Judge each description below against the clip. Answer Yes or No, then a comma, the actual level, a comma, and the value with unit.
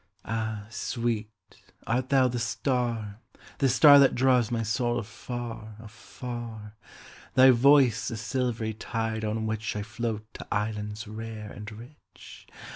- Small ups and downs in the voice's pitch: Yes, narrow, 2.3 semitones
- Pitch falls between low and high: No, low, 115 Hz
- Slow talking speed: Yes, slow, 120 wpm